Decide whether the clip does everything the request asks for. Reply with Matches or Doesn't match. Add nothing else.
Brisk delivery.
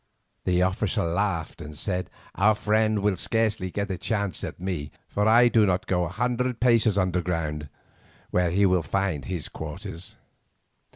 Doesn't match